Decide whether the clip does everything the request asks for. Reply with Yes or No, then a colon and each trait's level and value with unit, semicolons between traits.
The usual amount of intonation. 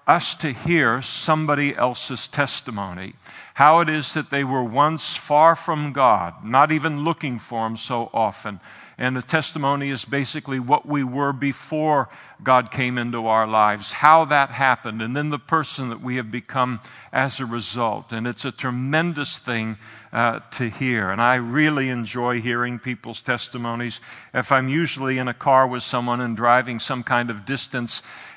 Yes: average, 3.4 semitones